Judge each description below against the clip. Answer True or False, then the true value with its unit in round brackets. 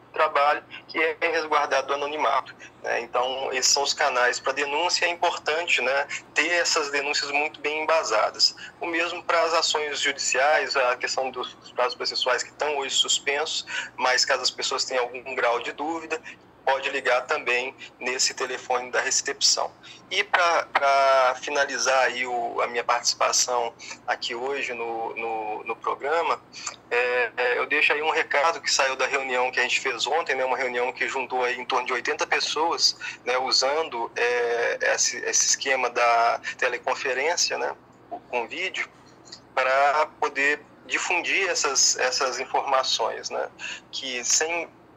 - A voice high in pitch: False (135 Hz)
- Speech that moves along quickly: False (150 wpm)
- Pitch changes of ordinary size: True (3.8 semitones)